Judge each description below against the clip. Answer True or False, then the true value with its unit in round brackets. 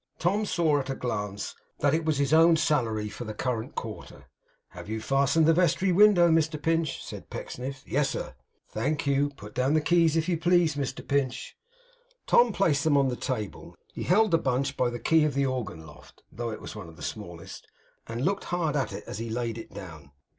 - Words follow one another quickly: True (210 wpm)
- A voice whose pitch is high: False (140 Hz)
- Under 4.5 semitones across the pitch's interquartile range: False (5.3 semitones)